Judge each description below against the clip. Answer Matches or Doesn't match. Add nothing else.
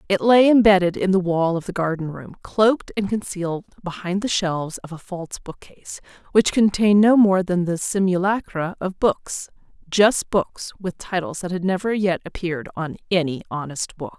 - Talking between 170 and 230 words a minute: Matches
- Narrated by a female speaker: Matches